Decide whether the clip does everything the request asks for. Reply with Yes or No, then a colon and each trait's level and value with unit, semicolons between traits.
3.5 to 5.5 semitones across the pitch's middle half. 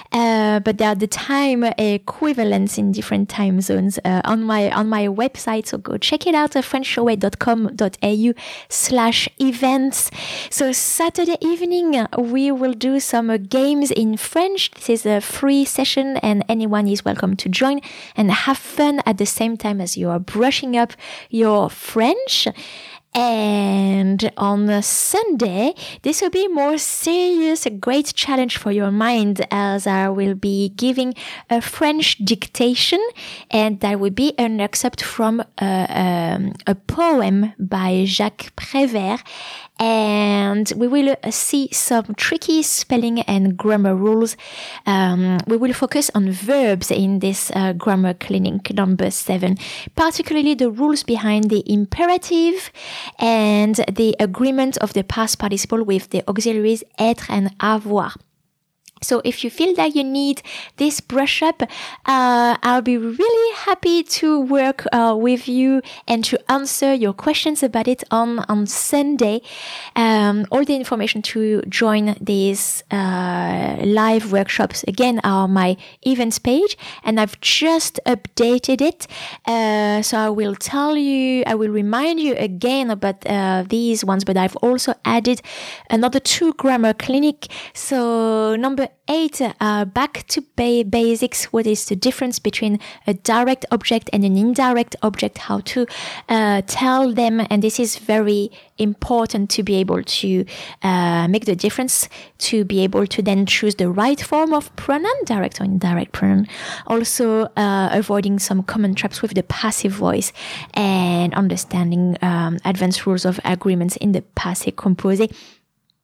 Yes: average, 4.6 semitones